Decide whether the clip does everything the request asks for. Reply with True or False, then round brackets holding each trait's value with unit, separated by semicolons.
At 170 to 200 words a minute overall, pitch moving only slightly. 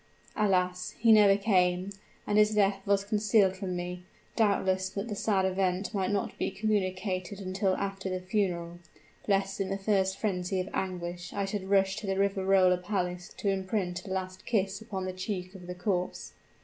True (175 wpm; 1.5 semitones)